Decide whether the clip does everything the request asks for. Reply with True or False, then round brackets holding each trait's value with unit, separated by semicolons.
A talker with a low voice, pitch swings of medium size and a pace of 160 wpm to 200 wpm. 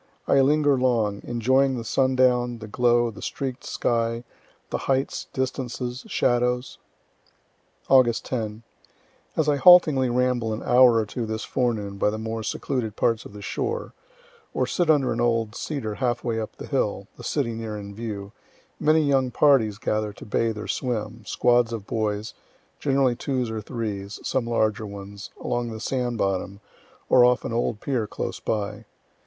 True (120 Hz; 3.0 semitones; 165 wpm)